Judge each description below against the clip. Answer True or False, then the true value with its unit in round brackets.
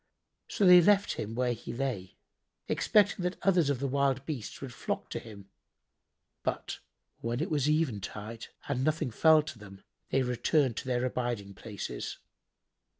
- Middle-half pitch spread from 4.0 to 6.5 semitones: True (5.1 semitones)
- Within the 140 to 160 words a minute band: True (155 wpm)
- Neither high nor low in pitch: False (130 Hz)